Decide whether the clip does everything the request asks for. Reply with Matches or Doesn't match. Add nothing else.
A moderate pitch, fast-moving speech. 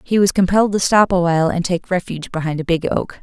Matches